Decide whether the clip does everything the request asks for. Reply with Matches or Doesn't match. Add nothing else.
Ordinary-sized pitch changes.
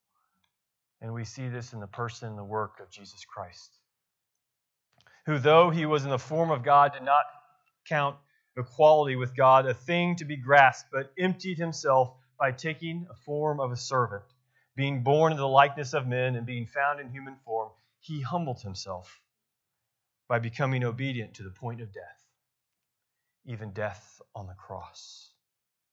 Matches